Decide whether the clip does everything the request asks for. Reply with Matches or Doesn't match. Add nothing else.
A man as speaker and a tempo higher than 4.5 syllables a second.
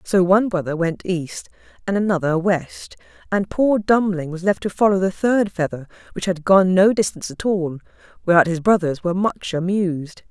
Doesn't match